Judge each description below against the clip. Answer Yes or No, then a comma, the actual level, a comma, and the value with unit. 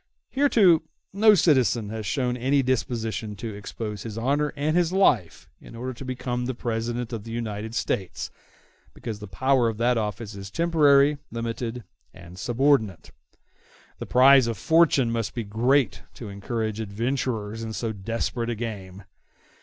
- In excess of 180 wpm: No, average, 155 wpm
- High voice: No, low, 115 Hz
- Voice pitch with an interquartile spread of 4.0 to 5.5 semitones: No, average, 3.6 semitones